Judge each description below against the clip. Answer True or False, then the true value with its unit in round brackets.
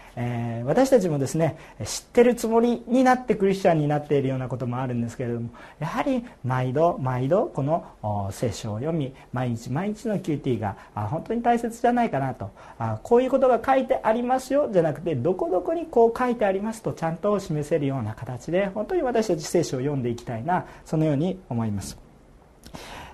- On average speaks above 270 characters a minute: True (395 characters per minute)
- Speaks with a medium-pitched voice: True (160 Hz)